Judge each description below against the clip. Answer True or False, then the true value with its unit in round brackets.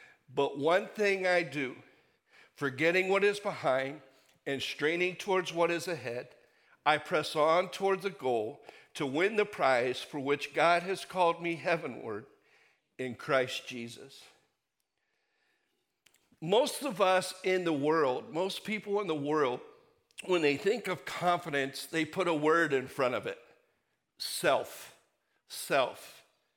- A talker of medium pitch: True (175 Hz)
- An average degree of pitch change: False (5.8 semitones)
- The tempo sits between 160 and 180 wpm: False (140 wpm)